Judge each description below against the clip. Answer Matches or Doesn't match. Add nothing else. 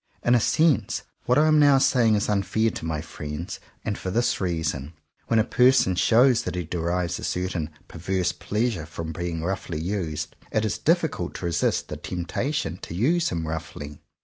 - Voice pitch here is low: Matches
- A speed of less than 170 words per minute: Doesn't match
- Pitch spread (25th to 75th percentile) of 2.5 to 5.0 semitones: Doesn't match